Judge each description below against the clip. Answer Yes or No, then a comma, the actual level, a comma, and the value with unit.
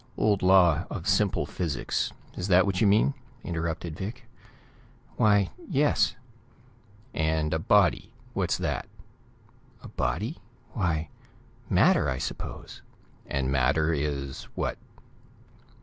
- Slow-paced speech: Yes, slow, 110 wpm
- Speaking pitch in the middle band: No, very low, 90 Hz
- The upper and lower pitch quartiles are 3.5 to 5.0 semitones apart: Yes, average, 4.7 semitones